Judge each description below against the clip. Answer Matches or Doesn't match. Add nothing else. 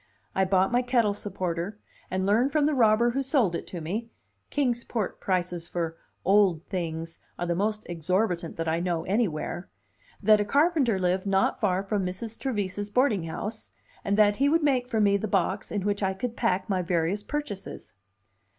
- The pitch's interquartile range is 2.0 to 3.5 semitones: Doesn't match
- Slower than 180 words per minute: Doesn't match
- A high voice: Matches